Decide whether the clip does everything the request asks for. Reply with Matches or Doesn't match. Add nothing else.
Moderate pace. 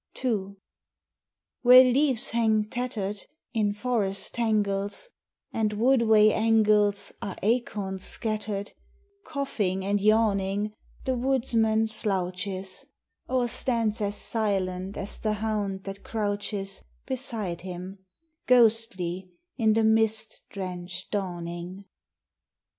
Doesn't match